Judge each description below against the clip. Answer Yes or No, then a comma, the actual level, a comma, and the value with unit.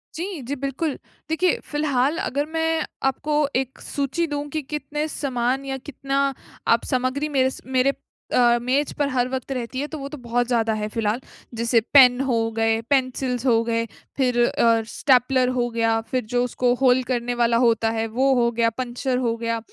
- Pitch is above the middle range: Yes, very high, 255 Hz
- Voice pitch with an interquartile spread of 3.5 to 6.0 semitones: No, average, 2.7 semitones